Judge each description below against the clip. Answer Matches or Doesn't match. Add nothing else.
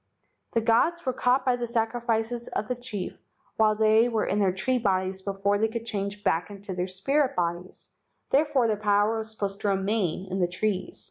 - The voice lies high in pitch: Matches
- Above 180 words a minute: Matches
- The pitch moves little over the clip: Doesn't match